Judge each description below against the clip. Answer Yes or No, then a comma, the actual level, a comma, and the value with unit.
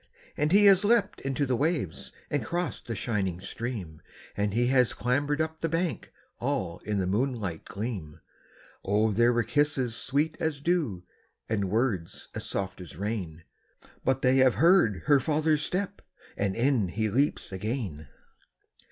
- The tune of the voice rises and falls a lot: Yes, wide, 6.7 semitones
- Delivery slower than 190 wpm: Yes, average, 155 wpm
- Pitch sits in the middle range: No, low, 120 Hz